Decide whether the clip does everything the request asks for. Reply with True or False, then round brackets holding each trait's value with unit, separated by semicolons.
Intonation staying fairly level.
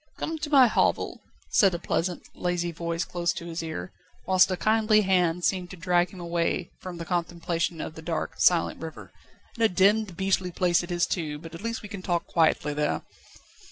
True (2.2 semitones)